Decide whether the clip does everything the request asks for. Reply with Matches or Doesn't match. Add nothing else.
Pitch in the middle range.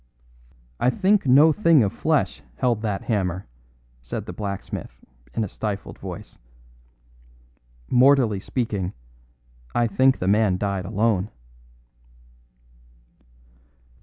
Doesn't match